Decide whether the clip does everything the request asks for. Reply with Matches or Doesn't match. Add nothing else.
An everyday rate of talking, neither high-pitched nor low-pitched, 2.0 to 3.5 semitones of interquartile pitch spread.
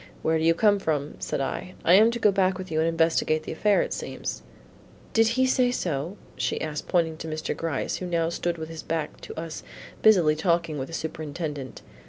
Doesn't match